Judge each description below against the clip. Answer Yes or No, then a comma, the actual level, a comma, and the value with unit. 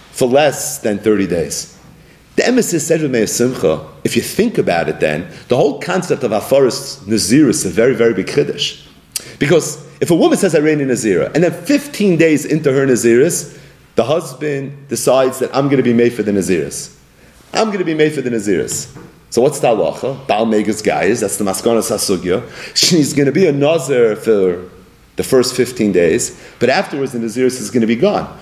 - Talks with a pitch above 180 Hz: No, low, 130 Hz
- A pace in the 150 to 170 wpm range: No, fast, 205 wpm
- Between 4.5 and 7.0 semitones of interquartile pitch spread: Yes, average, 4.9 semitones